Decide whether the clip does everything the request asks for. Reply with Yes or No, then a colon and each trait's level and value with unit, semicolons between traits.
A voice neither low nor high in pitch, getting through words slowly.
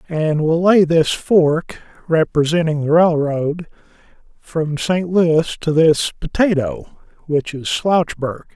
Yes: medium, 160 Hz; slow, 120 wpm